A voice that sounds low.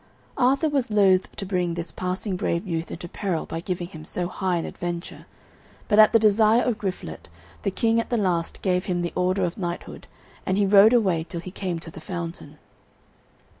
No: medium, 185 Hz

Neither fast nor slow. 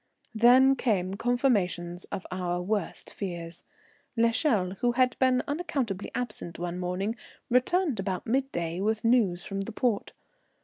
No: slow, 130 wpm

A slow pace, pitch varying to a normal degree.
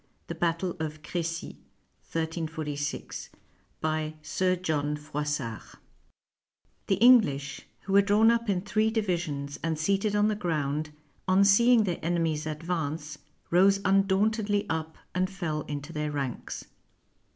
Yes: slow, 120 wpm; average, 4.6 semitones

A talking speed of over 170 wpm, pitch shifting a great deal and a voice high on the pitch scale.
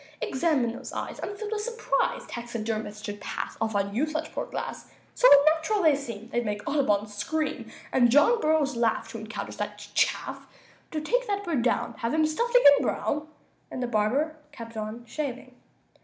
Yes: average, 180 wpm; wide, 5.7 semitones; very high, 270 Hz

